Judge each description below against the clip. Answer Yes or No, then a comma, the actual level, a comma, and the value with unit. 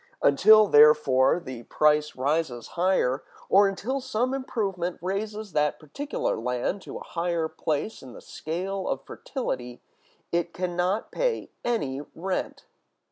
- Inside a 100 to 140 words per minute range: Yes, slow, 135 wpm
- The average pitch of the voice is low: No, medium, 175 Hz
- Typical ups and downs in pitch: No, wide, 5.7 semitones